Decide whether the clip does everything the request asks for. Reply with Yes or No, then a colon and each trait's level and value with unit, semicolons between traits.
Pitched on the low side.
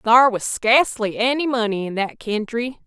No: high, 230 Hz